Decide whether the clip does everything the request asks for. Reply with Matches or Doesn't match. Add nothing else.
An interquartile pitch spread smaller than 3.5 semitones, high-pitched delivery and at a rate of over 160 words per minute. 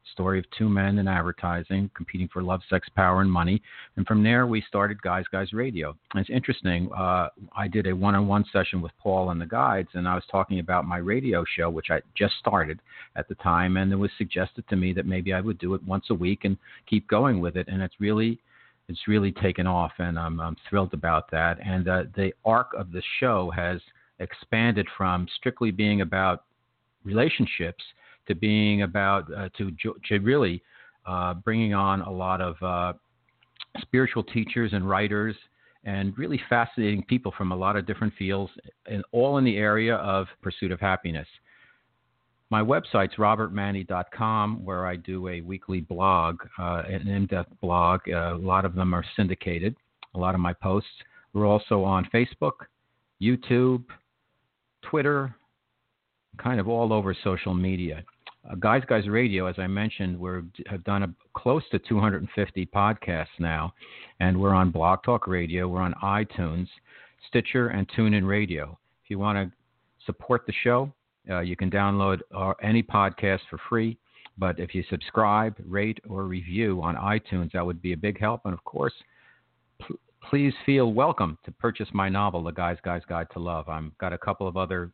Doesn't match